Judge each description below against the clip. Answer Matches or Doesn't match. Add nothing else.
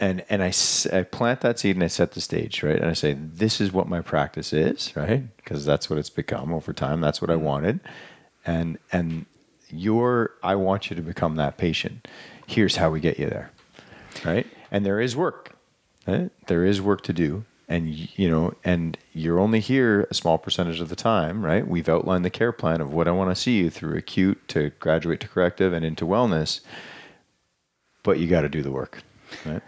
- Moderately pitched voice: Doesn't match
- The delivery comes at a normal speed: Doesn't match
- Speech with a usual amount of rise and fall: Matches